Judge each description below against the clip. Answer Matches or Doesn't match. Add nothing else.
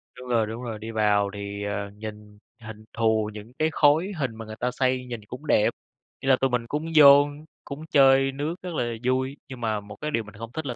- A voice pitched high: Doesn't match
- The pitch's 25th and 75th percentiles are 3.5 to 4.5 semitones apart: Matches